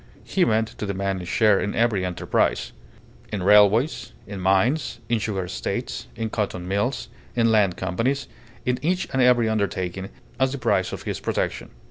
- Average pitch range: Yes, average, 3.9 semitones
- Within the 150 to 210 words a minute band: Yes, average, 165 wpm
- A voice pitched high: No, low, 105 Hz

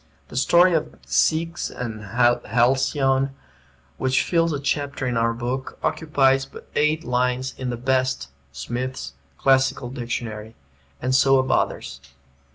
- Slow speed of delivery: Yes, slow, 130 wpm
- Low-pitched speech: Yes, low, 130 Hz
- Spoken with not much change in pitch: Yes, narrow, 2.1 semitones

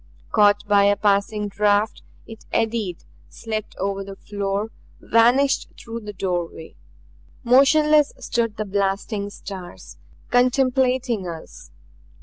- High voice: Yes, high, 210 Hz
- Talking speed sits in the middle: No, slow, 110 wpm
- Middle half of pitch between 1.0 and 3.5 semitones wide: Yes, average, 3.0 semitones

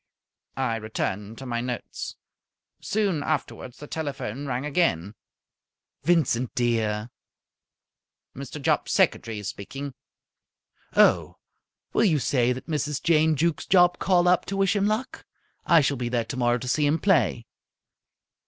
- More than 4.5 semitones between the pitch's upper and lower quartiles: Yes, wide, 5.6 semitones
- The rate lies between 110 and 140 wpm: Yes, slow, 135 wpm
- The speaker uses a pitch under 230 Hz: Yes, medium, 140 Hz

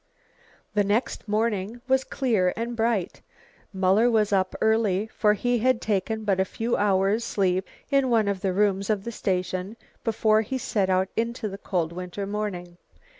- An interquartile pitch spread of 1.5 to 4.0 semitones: Yes, average, 3.1 semitones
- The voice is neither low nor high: No, high, 210 Hz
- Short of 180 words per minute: Yes, average, 170 wpm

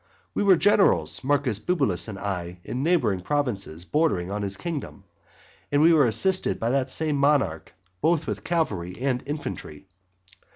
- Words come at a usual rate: Yes, average, 155 wpm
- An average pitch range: No, wide, 8.1 semitones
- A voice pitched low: Yes, low, 130 Hz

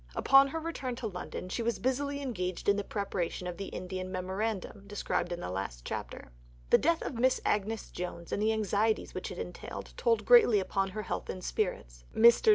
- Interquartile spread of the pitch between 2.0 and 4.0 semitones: No, average, 4.9 semitones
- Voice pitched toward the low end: No, high, 205 Hz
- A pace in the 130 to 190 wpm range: No, fast, 205 wpm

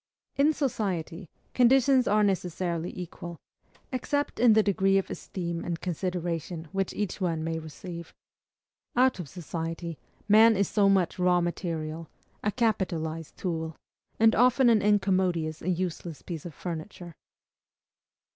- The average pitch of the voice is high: No, medium, 180 Hz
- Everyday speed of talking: No, slow, 130 wpm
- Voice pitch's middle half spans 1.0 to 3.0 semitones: No, average, 3.8 semitones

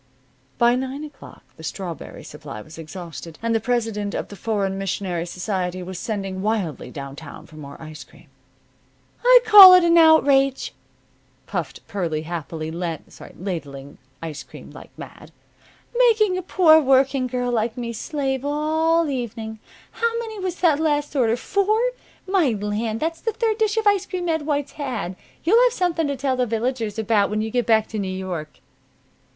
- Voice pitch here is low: No, high, 235 Hz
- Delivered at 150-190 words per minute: Yes, average, 170 wpm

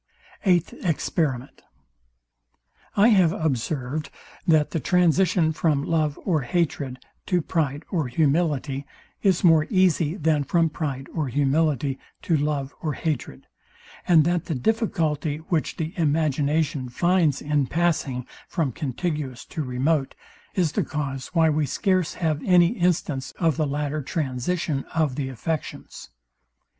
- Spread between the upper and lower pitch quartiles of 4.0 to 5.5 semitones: No, average, 3.3 semitones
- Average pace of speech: No, slow, 130 wpm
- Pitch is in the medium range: Yes, medium, 155 Hz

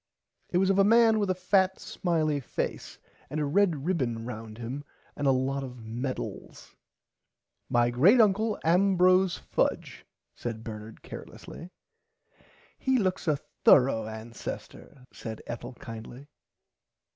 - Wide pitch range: Yes, wide, 7.8 semitones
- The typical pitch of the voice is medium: Yes, medium, 145 Hz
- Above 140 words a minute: No, slow, 135 wpm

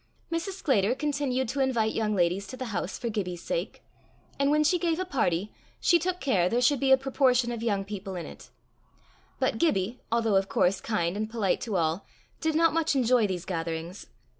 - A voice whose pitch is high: Yes, high, 230 Hz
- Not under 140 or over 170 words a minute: No, average, 200 wpm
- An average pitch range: No, wide, 6.3 semitones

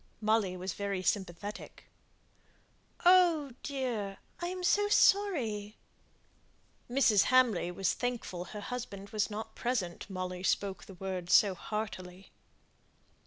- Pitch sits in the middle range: No, high, 210 Hz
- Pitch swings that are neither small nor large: Yes, average, 4.9 semitones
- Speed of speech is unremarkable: No, slow, 115 wpm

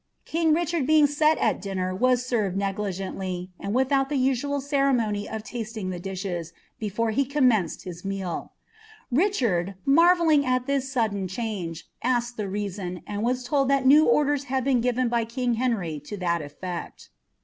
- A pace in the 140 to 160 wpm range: Yes, average, 150 wpm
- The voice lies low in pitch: No, high, 235 Hz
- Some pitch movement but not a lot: No, wide, 5.8 semitones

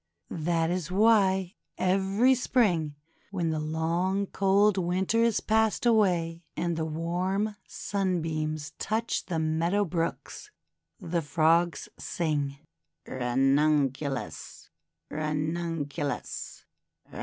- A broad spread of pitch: No, average, 3.8 semitones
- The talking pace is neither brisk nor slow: No, slow, 95 wpm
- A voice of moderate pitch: Yes, medium, 170 Hz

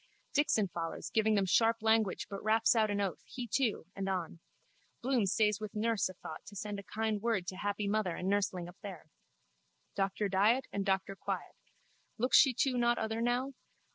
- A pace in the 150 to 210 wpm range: Yes, average, 190 wpm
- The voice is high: Yes, high, 210 Hz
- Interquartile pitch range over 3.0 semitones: No, average, 2.7 semitones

